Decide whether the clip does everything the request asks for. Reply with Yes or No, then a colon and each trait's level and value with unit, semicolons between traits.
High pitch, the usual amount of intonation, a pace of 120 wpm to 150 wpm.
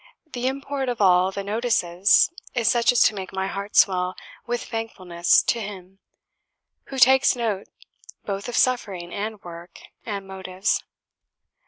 Yes: high, 200 Hz; average, 4.2 semitones; average, 145 wpm